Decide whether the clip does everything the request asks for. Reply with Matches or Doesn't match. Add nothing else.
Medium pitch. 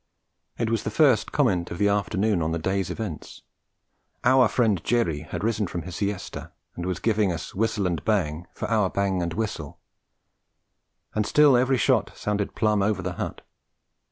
Doesn't match